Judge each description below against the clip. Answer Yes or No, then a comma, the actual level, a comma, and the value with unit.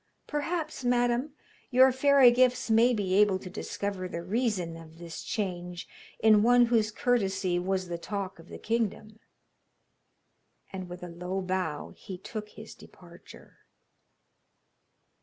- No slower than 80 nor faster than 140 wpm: Yes, slow, 135 wpm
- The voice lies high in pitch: Yes, high, 200 Hz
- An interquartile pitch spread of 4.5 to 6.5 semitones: Yes, average, 5.1 semitones